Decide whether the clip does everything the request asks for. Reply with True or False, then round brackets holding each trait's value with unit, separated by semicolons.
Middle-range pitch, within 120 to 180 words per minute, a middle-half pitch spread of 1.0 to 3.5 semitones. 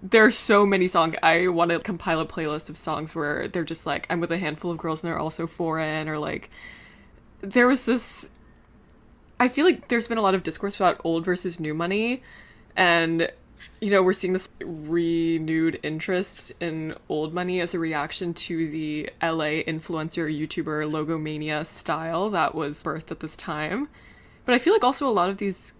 False (165 Hz; 190 wpm; 3.1 semitones)